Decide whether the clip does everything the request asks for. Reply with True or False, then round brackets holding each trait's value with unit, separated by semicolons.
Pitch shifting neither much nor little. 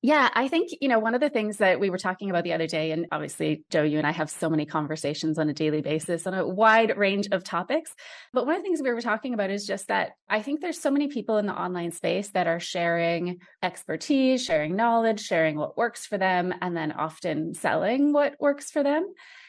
False (7.6 semitones)